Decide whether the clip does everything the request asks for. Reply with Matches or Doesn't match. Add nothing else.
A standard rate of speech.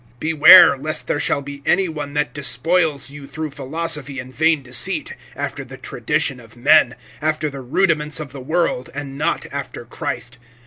Matches